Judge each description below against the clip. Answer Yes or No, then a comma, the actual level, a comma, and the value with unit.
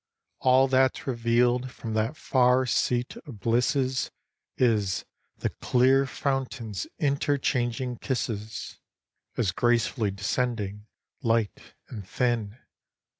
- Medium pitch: No, low, 120 Hz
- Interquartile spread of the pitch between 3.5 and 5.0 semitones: No, average, 2.8 semitones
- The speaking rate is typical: No, slow, 100 wpm